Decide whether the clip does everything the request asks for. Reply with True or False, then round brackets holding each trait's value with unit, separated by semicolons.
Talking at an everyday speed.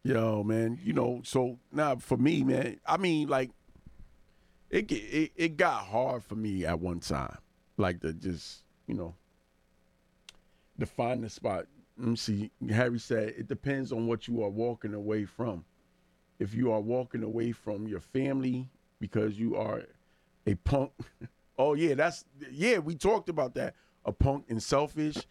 True (170 wpm)